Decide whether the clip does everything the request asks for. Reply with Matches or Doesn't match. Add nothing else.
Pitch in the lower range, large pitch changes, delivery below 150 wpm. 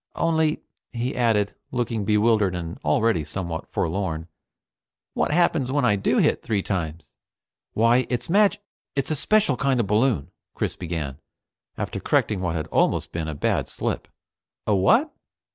Doesn't match